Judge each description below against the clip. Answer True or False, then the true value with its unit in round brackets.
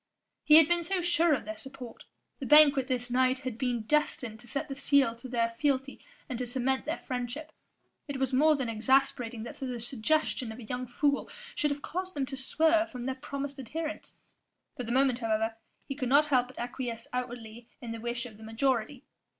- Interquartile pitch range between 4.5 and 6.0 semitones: False (3.0 semitones)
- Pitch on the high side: True (260 Hz)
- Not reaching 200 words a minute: False (205 wpm)